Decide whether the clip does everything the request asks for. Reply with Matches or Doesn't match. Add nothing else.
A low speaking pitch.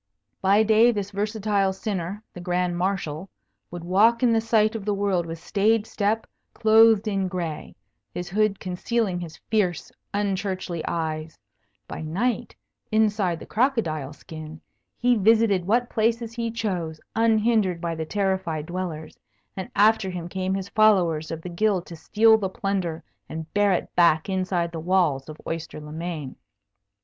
Doesn't match